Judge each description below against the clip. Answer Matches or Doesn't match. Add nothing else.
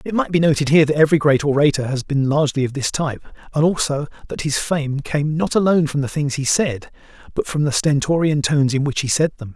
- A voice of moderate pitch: Matches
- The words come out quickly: Matches